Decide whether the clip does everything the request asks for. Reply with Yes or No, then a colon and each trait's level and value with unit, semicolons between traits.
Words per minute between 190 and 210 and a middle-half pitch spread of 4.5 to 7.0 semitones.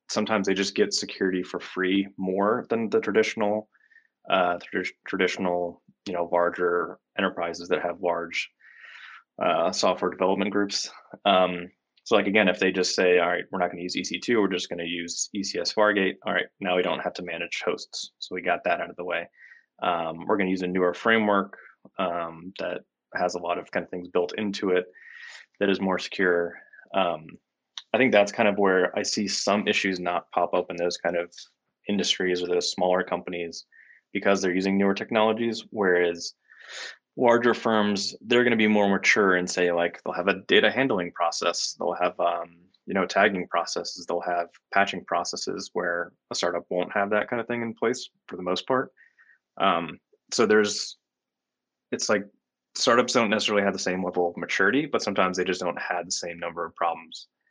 No: average, 195 wpm; average, 2.7 semitones